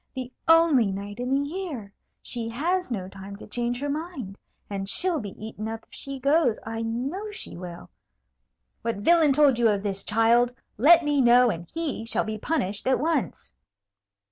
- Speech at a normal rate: Yes, average, 180 wpm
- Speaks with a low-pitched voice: No, high, 240 Hz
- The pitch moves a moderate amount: No, wide, 5.9 semitones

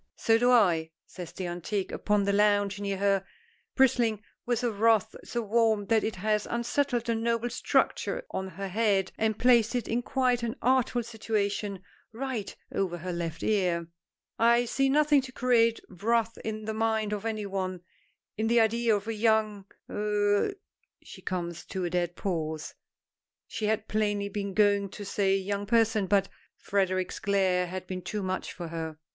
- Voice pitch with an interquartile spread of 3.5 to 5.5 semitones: No, average, 3.1 semitones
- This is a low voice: No, high, 210 Hz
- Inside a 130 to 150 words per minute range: No, average, 175 wpm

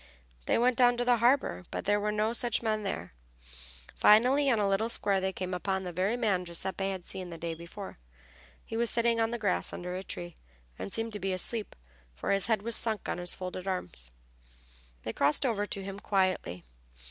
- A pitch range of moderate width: Yes, average, 3.9 semitones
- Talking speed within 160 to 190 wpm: No, fast, 205 wpm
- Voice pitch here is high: Yes, high, 200 Hz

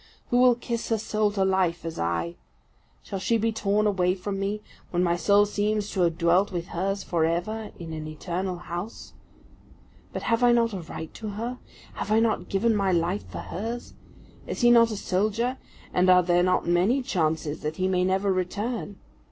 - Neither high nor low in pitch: No, high, 195 Hz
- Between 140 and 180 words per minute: No, average, 195 wpm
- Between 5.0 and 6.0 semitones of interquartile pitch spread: No, average, 3.8 semitones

